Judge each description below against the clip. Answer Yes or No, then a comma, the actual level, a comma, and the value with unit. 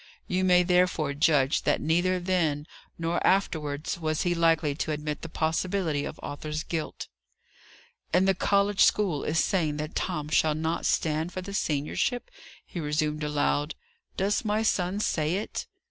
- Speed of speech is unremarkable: Yes, average, 155 wpm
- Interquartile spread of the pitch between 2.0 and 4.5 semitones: Yes, average, 3.4 semitones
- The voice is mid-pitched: Yes, medium, 165 Hz